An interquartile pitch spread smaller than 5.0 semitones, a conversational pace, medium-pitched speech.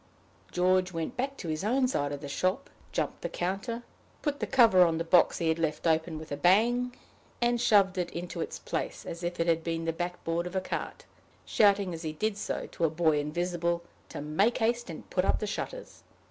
No: average, 4.2 semitones; fast, 215 wpm; medium, 175 Hz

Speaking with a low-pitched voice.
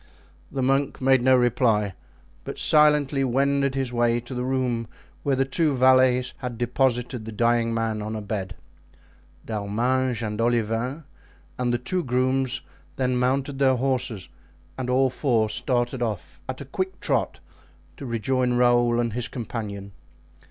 Yes: low, 125 Hz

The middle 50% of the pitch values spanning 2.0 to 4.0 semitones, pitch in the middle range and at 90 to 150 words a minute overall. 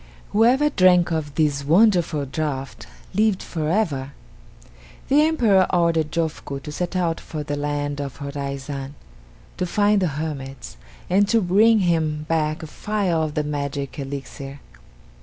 No: average, 4.6 semitones; medium, 155 Hz; average, 140 wpm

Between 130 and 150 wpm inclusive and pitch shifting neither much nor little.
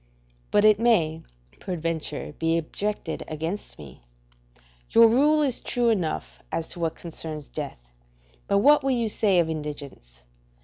No: average, 140 wpm; wide, 6.4 semitones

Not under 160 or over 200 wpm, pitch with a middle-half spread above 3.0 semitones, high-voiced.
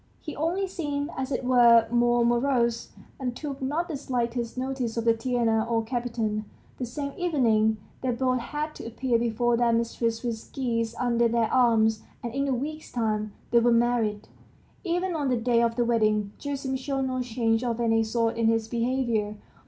No: average, 180 wpm; narrow, 2.5 semitones; high, 240 Hz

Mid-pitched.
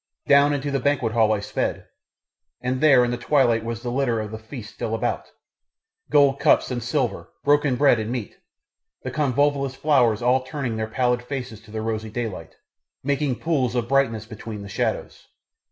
No: low, 125 Hz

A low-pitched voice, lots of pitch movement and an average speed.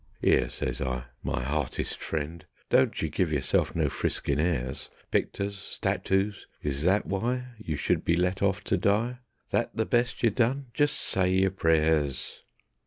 Yes: very low, 95 Hz; wide, 5.7 semitones; average, 160 wpm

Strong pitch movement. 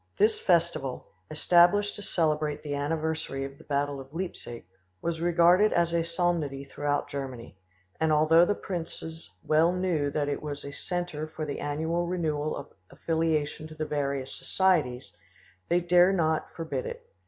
No: average, 3.1 semitones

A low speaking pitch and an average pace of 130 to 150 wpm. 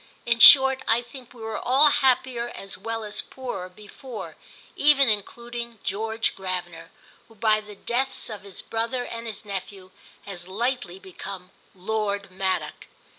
No: high, 220 Hz; average, 145 wpm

